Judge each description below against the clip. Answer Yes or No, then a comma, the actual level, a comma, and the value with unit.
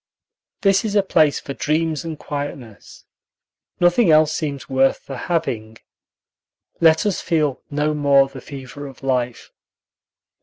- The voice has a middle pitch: Yes, medium, 145 Hz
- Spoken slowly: Yes, slow, 130 wpm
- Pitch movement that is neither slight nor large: Yes, average, 3.2 semitones